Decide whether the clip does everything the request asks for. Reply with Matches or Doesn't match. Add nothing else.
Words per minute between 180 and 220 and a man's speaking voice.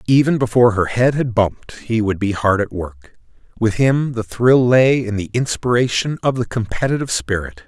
Matches